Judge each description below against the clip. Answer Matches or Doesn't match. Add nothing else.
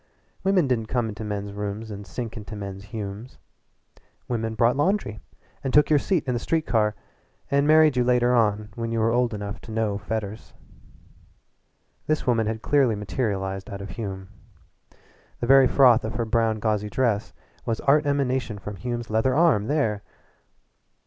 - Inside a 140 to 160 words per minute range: Doesn't match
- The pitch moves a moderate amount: Matches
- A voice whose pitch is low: Matches